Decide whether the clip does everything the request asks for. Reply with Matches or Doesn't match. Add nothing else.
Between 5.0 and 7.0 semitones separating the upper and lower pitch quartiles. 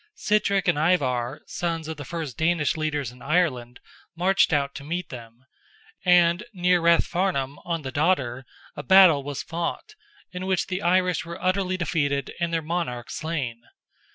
Doesn't match